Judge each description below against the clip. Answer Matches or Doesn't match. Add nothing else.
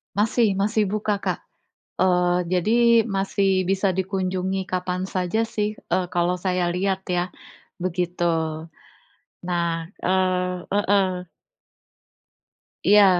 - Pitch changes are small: Matches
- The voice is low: Doesn't match